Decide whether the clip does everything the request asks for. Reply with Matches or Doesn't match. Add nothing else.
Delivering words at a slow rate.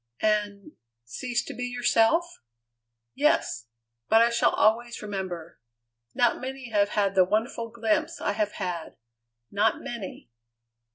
Matches